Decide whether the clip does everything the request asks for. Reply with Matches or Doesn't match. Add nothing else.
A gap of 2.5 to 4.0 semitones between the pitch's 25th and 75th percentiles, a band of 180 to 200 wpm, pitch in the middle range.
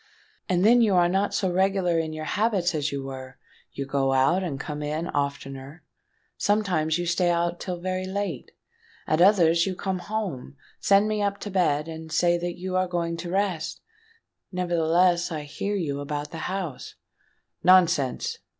Doesn't match